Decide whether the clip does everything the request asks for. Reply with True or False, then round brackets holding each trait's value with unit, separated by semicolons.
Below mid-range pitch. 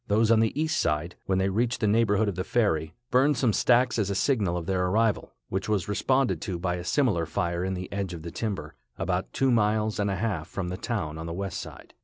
True (100 Hz)